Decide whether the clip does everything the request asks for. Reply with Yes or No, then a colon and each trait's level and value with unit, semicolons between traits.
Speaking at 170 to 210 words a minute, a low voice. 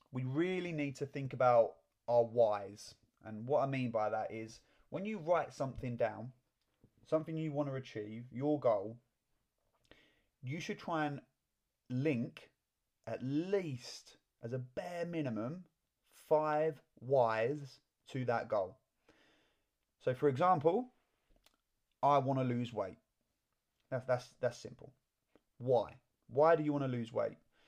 No: slow, 135 wpm; low, 130 Hz